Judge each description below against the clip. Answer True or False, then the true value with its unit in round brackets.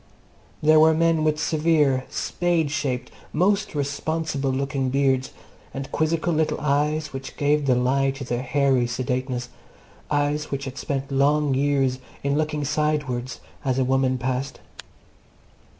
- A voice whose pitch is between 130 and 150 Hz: True (140 Hz)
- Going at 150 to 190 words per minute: False (135 wpm)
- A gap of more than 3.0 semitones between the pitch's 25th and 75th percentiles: False (2.5 semitones)